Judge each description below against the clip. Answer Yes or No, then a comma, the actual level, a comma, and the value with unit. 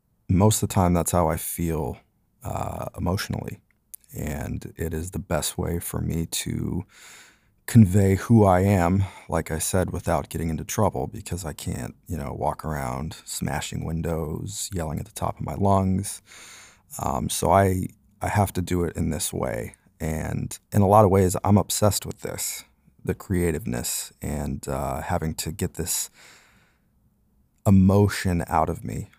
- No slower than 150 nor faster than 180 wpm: Yes, average, 160 wpm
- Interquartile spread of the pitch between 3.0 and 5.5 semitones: Yes, average, 3.8 semitones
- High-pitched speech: No, very low, 90 Hz